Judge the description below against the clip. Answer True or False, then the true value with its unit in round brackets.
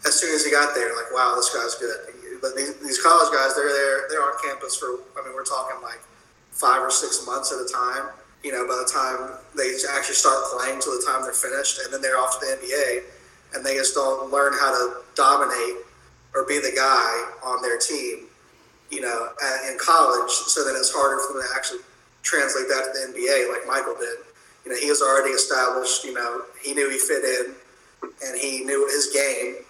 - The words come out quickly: True (220 wpm)